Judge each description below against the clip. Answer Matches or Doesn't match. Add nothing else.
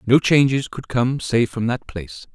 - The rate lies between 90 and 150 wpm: Doesn't match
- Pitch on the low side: Matches